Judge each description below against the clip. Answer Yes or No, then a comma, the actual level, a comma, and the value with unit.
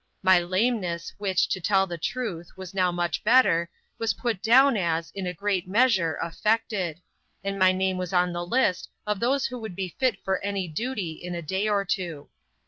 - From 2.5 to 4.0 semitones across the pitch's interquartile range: Yes, average, 3.5 semitones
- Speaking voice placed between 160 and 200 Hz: Yes, high, 190 Hz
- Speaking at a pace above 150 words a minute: Yes, average, 195 wpm